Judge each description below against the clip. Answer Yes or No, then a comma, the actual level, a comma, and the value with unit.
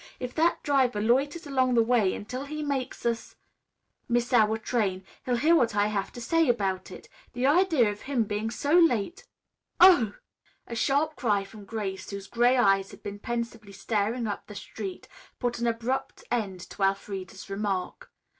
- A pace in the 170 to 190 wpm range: Yes, average, 175 wpm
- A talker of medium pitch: No, high, 230 Hz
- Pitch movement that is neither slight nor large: Yes, average, 4.2 semitones